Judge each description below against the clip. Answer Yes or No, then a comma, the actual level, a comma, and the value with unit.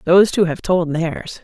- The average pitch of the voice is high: No, medium, 170 Hz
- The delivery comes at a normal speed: No, fast, 210 wpm